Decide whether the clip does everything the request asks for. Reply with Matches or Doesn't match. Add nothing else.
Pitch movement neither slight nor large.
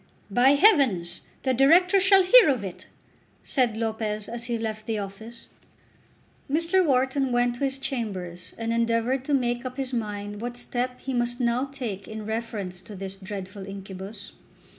Matches